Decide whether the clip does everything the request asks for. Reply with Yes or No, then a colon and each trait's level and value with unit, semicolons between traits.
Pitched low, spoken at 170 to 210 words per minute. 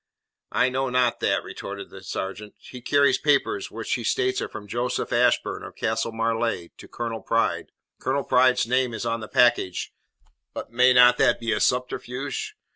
Yes: low, 120 Hz; average, 175 wpm